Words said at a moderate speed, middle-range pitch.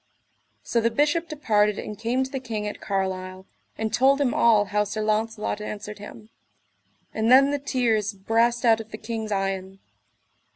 No: average, 170 wpm; high, 220 Hz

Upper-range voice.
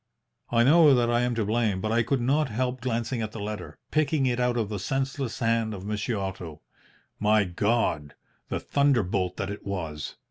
No: low, 115 Hz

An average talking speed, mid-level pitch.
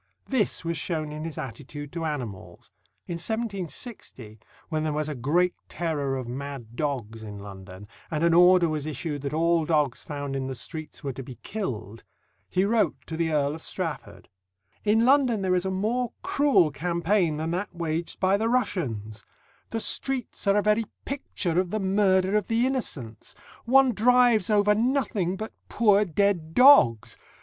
Yes: average, 170 wpm; medium, 170 Hz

